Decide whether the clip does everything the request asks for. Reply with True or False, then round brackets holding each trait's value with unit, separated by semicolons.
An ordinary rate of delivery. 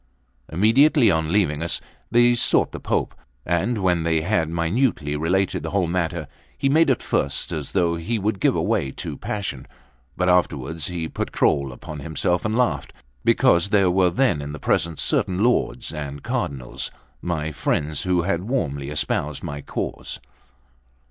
True (160 wpm)